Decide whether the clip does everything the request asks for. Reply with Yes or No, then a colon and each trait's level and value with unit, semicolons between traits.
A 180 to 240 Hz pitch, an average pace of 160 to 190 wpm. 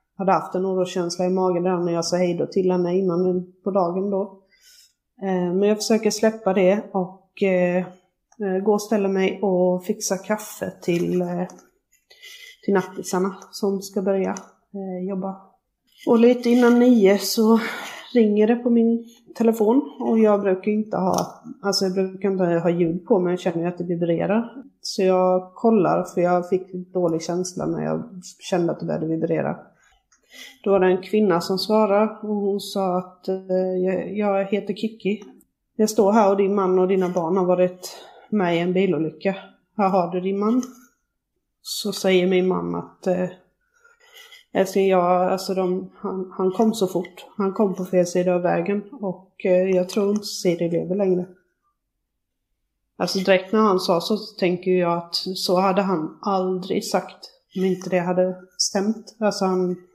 Yes: high, 190 Hz; average, 165 wpm